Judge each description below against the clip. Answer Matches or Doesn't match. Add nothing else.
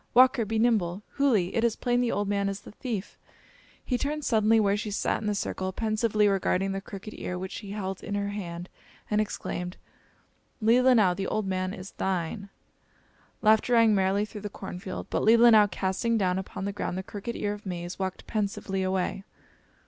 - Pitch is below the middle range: Doesn't match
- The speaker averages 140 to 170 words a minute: Doesn't match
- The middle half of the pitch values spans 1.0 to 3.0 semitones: Matches